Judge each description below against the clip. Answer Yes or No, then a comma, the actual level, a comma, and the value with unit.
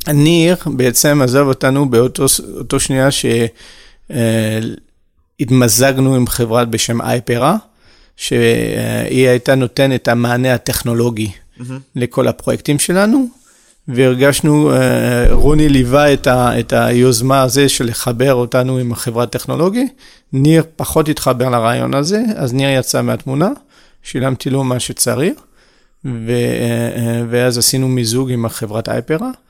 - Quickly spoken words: No, average, 105 wpm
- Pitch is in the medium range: No, low, 130 Hz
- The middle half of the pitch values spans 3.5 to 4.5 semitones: No, average, 2.9 semitones